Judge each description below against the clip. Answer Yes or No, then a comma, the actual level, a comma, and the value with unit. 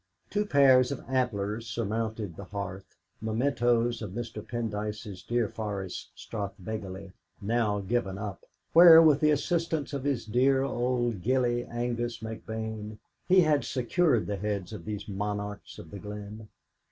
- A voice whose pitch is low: Yes, low, 110 Hz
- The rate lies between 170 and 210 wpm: No, average, 140 wpm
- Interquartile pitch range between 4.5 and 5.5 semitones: No, average, 3.5 semitones